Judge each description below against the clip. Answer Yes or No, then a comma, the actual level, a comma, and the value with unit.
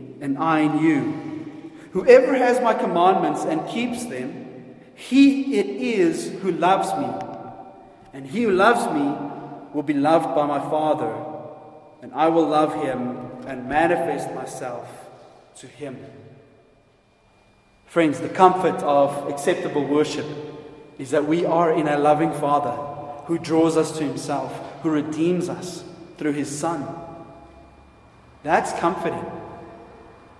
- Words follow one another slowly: Yes, slow, 130 wpm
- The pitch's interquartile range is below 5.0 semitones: Yes, average, 2.9 semitones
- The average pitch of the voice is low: No, medium, 155 Hz